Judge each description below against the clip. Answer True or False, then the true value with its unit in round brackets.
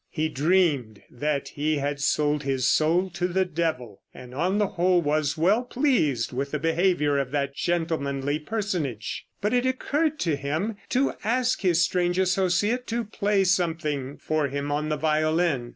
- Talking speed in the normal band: True (165 wpm)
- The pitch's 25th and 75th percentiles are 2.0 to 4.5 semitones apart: False (4.9 semitones)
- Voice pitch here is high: False (160 Hz)